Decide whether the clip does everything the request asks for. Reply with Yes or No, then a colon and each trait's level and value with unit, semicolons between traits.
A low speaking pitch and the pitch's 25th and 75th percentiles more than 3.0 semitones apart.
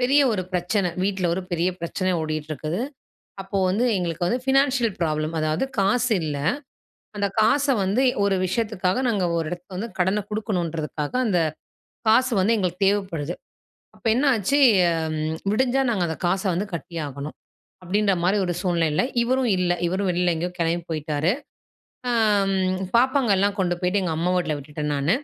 No: medium, 185 Hz; average, 4.2 semitones